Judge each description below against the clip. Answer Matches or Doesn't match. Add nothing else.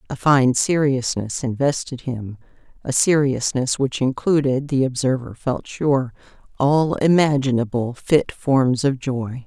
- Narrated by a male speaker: Doesn't match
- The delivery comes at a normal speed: Doesn't match